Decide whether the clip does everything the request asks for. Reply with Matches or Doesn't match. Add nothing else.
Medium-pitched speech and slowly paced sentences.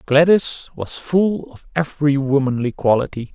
Matches